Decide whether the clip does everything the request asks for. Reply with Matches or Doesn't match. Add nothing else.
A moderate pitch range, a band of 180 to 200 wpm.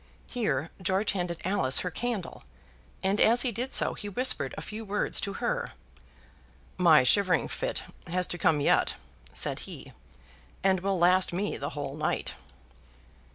Doesn't match